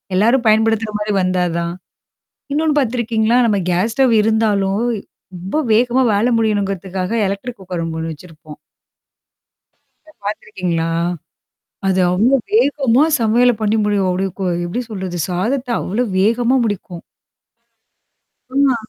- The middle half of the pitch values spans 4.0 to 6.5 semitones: Yes, average, 4.5 semitones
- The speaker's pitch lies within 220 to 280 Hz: No, high, 210 Hz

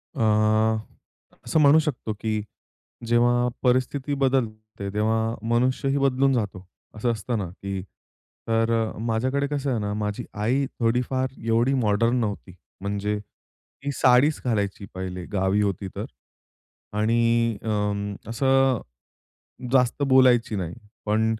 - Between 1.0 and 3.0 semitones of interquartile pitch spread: No, average, 3.8 semitones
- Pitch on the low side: Yes, low, 115 Hz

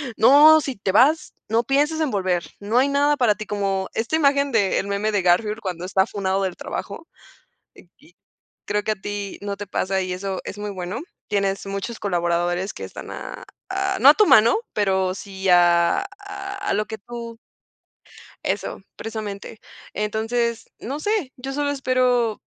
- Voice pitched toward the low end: No, high, 210 Hz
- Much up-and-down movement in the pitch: Yes, wide, 5.7 semitones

